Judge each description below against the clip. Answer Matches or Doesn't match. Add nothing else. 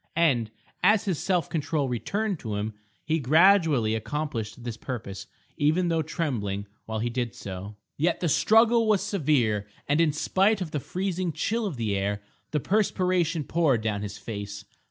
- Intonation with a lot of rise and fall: Matches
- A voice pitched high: Doesn't match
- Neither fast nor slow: Matches